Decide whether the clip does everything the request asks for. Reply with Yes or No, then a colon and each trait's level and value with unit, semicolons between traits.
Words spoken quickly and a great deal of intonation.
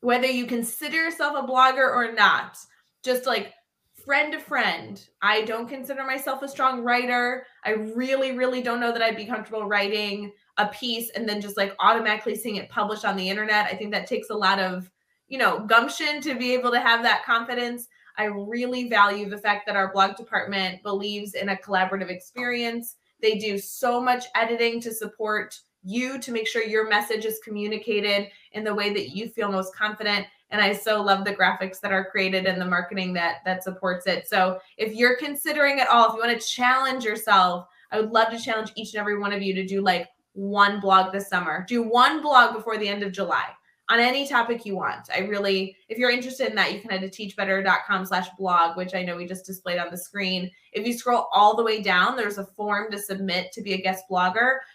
No: fast, 215 wpm; average, 3.6 semitones